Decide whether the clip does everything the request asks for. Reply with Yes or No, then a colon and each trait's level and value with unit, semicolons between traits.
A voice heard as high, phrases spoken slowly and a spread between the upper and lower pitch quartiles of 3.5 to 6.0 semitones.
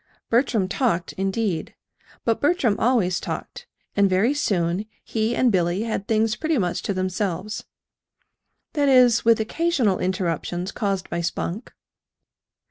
Yes: high, 210 Hz; slow, 130 wpm; average, 4.3 semitones